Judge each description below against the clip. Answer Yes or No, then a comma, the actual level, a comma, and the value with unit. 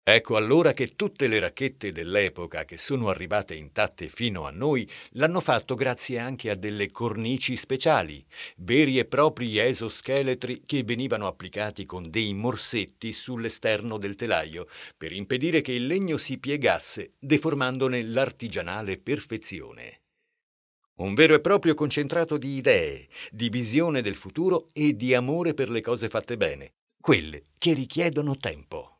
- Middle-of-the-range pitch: No, low, 125 Hz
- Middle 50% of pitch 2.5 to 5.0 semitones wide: No, wide, 5.5 semitones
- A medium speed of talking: Yes, average, 140 wpm